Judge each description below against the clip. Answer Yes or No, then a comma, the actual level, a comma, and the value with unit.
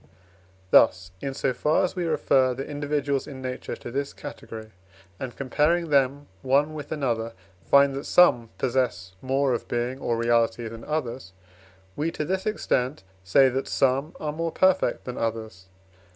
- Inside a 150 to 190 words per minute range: Yes, average, 160 wpm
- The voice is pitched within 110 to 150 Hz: Yes, low, 135 Hz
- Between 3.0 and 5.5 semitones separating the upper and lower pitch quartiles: Yes, average, 3.8 semitones